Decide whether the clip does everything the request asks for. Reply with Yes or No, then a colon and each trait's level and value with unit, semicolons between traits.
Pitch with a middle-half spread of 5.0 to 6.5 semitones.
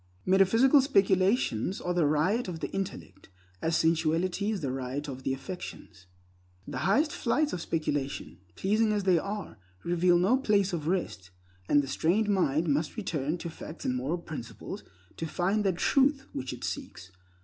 Yes: wide, 5.6 semitones